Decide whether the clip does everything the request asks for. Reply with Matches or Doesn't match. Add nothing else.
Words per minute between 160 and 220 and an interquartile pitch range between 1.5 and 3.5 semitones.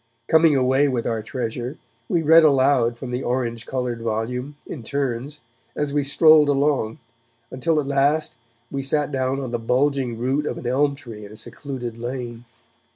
Matches